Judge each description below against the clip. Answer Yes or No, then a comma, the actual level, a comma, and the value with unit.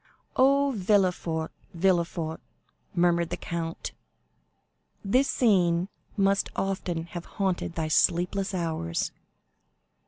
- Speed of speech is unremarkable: No, slow, 90 wpm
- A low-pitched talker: No, medium, 175 Hz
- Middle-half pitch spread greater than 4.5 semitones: No, average, 2.7 semitones